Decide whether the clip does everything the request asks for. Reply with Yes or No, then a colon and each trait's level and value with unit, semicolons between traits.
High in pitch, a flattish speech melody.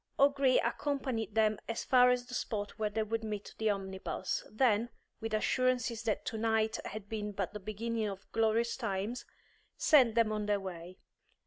Yes: high, 220 Hz; narrow, 2.3 semitones